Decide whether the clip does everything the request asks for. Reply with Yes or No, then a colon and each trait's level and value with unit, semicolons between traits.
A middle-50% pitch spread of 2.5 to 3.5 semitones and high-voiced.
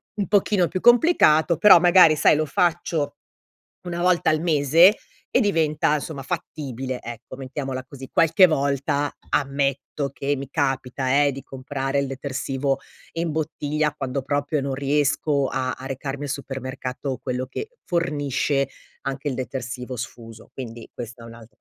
No: average, 2.8 semitones; medium, 140 Hz